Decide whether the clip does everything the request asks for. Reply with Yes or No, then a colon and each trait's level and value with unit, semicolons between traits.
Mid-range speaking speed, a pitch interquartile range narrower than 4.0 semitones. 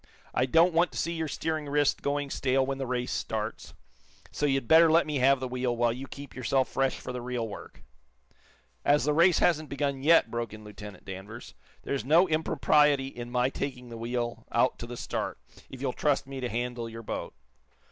No: fast, 210 wpm; average, 3.4 semitones